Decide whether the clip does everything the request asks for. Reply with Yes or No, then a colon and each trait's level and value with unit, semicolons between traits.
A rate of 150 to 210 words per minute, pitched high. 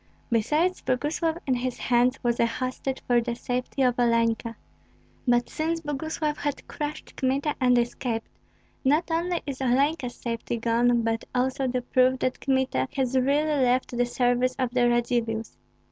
Yes: average, 155 wpm; very high, 255 Hz